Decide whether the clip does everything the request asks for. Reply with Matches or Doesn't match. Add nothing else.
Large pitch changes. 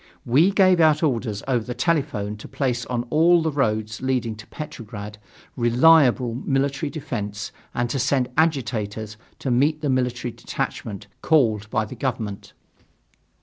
Doesn't match